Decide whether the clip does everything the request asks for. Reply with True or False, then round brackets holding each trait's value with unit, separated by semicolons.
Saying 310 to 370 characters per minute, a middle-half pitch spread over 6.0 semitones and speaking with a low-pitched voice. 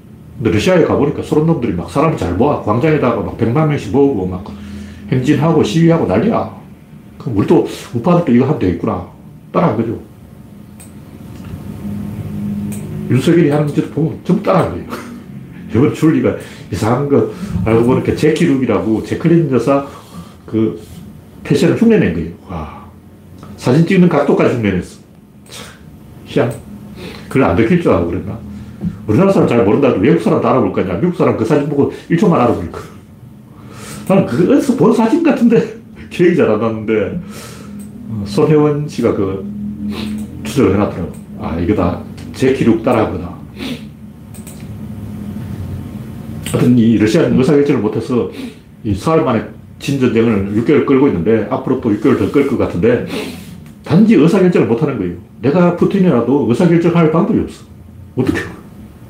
True (315 characters per minute; 6.7 semitones; 115 Hz)